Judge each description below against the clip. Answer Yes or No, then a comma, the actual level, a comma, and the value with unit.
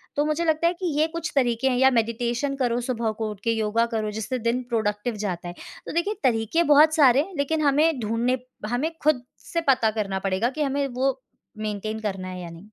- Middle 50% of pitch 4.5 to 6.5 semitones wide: Yes, average, 4.8 semitones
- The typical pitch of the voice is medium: No, high, 245 Hz